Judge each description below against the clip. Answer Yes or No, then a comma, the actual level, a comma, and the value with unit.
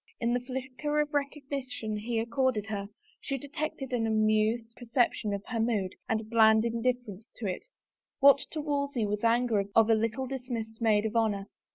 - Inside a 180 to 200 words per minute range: Yes, average, 190 wpm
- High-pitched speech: Yes, high, 230 Hz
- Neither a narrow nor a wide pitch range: Yes, average, 3.2 semitones